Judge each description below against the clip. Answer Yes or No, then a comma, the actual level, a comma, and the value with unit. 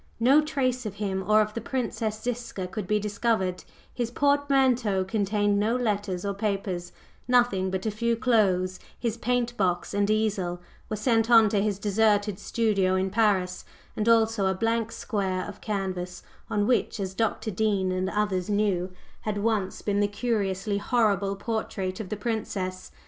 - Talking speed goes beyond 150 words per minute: Yes, average, 165 wpm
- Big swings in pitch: No, average, 3.1 semitones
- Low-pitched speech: No, high, 210 Hz